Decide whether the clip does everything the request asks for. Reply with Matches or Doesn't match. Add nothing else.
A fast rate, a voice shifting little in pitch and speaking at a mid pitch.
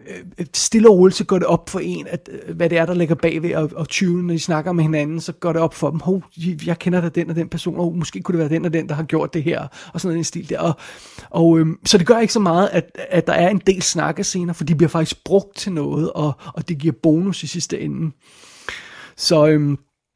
Matches